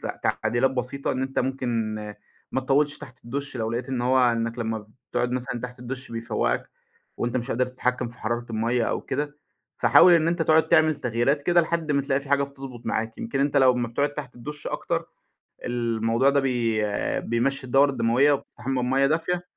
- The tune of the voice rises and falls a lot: No, average, 2.9 semitones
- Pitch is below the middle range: Yes, low, 130 Hz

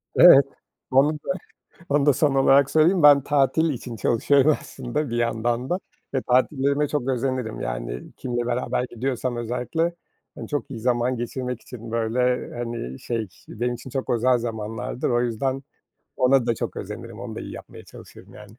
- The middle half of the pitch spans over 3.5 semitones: No, narrow, 2.5 semitones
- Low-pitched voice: Yes, low, 125 Hz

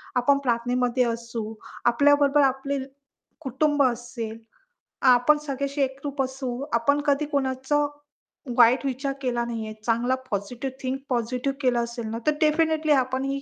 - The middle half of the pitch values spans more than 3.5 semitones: No, average, 2.7 semitones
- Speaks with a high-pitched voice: Yes, very high, 260 Hz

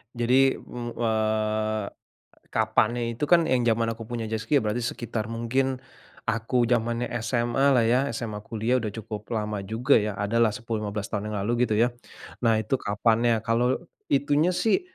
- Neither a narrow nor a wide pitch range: No, narrow, 2.0 semitones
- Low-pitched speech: Yes, low, 115 Hz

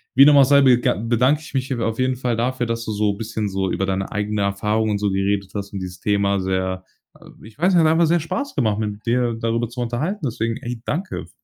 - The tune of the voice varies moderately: Yes, average, 4.1 semitones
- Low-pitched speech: Yes, low, 115 Hz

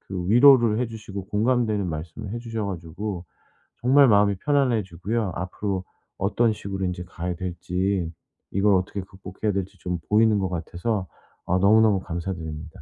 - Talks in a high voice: No, low, 100 Hz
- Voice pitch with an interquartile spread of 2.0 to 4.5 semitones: Yes, average, 3.4 semitones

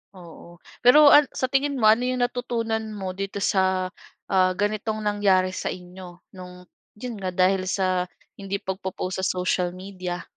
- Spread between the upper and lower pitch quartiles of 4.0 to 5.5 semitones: No, average, 3.0 semitones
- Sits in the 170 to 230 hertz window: Yes, high, 190 Hz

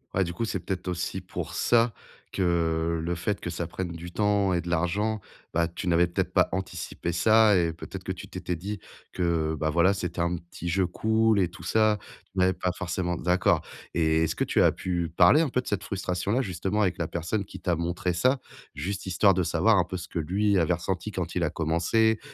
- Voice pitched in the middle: No, very low, 90 Hz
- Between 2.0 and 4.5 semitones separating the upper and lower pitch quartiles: Yes, average, 2.9 semitones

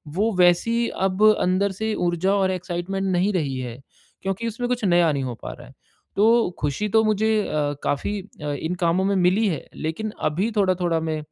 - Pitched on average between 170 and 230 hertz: Yes, medium, 185 Hz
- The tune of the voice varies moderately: Yes, average, 4.1 semitones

